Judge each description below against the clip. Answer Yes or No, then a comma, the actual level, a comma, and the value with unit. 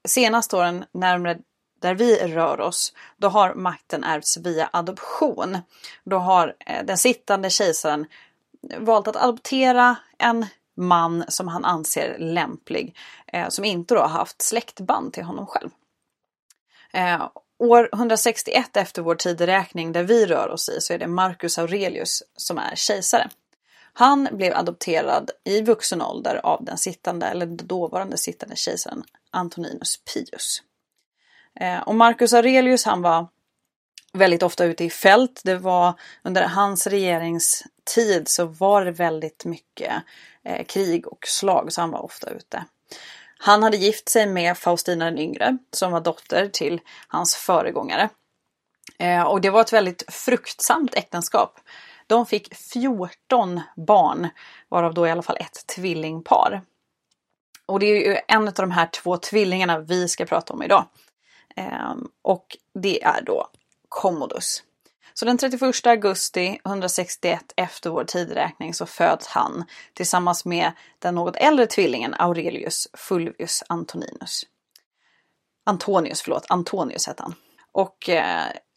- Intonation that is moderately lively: Yes, average, 4.5 semitones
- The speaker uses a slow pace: No, average, 135 wpm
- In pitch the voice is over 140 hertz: Yes, medium, 185 Hz